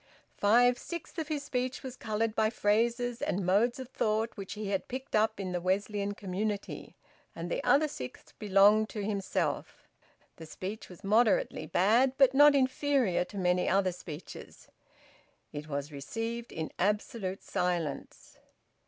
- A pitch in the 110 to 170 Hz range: No, high, 210 Hz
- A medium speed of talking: Yes, average, 150 wpm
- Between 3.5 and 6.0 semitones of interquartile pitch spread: Yes, average, 4.5 semitones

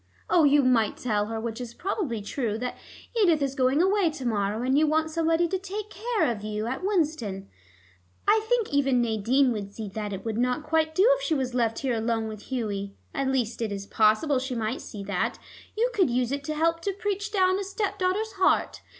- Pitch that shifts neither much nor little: No, wide, 7.4 semitones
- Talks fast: Yes, fast, 215 wpm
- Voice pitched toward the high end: Yes, very high, 265 Hz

